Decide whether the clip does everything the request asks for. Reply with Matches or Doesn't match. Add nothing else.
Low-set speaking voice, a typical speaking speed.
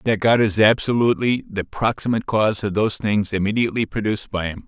Matches